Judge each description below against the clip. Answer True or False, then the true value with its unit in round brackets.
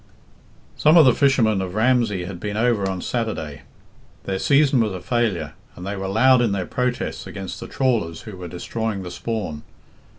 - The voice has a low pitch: True (105 Hz)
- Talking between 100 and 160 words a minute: False (185 wpm)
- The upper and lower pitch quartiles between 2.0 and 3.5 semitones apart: False (4.7 semitones)